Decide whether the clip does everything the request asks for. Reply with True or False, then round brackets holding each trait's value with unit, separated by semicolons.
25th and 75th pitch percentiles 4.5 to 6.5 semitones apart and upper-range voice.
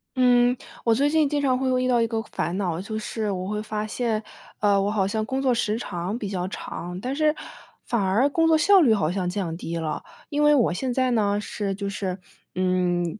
True (5.1 semitones; 215 Hz)